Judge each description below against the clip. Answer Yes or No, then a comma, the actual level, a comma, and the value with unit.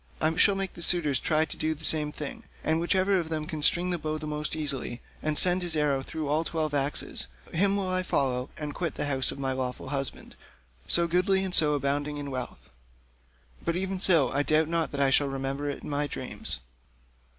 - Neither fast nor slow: No, fast, 215 wpm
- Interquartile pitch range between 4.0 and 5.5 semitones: No, average, 3.3 semitones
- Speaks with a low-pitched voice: No, medium, 155 Hz